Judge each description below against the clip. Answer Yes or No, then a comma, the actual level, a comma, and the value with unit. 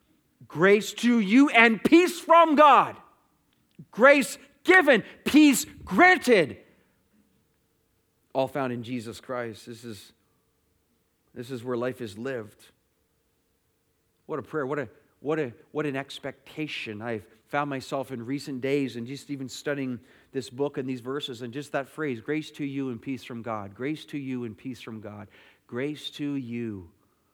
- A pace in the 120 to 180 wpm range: Yes, average, 155 wpm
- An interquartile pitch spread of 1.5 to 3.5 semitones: No, average, 4.4 semitones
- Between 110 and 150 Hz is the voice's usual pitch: Yes, low, 135 Hz